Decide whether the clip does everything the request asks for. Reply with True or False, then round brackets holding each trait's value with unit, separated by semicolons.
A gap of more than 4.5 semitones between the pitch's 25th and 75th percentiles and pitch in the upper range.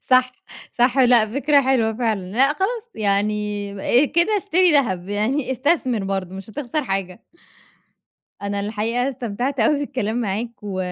True (5.0 semitones; 240 Hz)